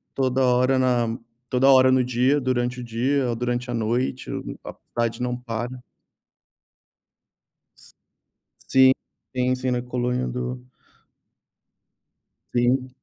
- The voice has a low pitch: Yes, low, 125 Hz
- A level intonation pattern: Yes, narrow, 1.0 semitones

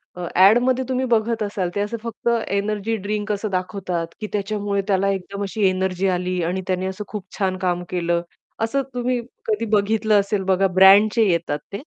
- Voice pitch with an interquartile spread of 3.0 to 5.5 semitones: No, narrow, 2.5 semitones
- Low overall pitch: No, high, 200 Hz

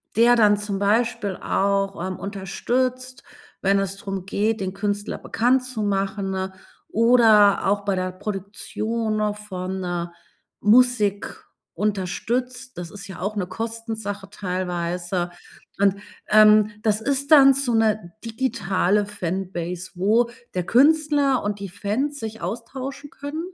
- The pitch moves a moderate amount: Yes, average, 3.4 semitones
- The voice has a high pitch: Yes, high, 205 Hz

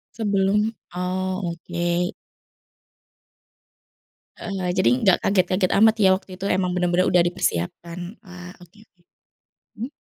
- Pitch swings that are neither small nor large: No, narrow, 1.6 semitones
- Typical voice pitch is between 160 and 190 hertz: Yes, medium, 185 Hz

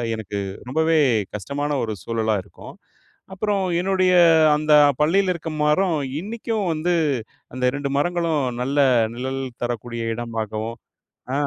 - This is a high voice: No, medium, 145 Hz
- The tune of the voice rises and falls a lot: Yes, wide, 7.0 semitones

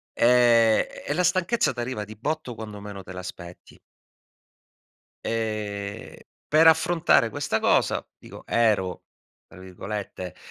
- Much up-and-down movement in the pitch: Yes, wide, 6.1 semitones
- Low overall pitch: Yes, low, 110 Hz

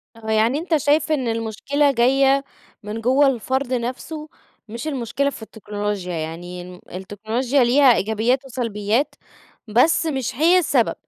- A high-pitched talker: Yes, high, 245 Hz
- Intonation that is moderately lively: Yes, average, 4.4 semitones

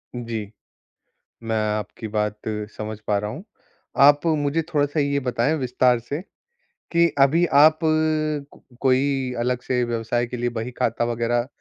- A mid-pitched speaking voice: No, low, 125 Hz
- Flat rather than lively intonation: No, average, 3.6 semitones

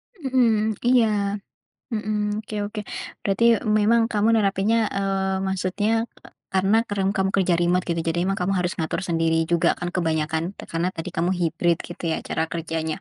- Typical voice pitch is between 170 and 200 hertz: Yes, high, 190 Hz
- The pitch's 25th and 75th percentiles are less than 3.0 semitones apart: No, average, 3.5 semitones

